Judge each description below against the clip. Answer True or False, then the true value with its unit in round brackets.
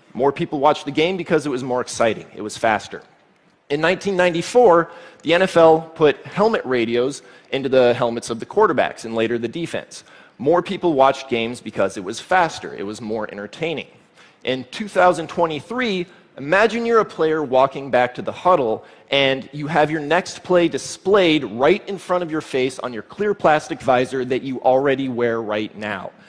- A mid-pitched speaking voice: True (150 Hz)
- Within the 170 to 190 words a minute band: True (175 wpm)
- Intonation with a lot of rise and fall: True (5.7 semitones)